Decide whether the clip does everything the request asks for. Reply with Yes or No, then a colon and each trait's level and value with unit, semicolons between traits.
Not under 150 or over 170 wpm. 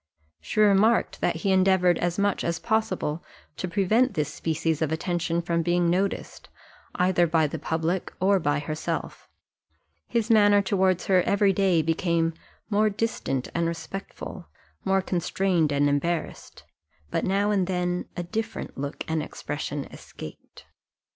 No: average, 140 wpm